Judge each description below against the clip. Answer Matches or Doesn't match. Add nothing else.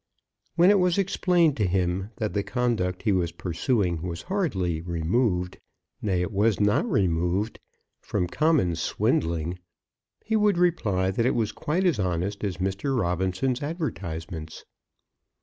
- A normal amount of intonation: Doesn't match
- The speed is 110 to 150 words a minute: Matches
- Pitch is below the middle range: Matches